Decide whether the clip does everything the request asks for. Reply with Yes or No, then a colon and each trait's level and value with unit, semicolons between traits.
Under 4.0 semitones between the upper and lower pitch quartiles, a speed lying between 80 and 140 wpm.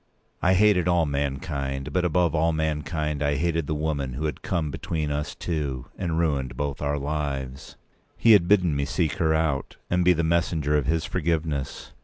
No: average, 2.9 semitones; average, 185 wpm